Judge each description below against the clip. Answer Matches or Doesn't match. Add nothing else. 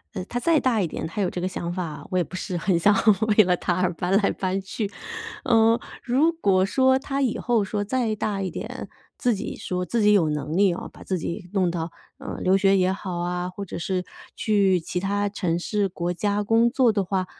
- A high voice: Matches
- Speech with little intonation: Doesn't match